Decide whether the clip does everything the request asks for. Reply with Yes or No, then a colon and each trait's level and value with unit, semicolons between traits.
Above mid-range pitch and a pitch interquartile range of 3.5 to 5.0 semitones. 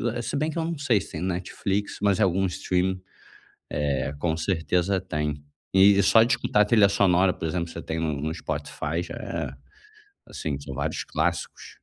No: very low, 90 Hz; average, 4.1 semitones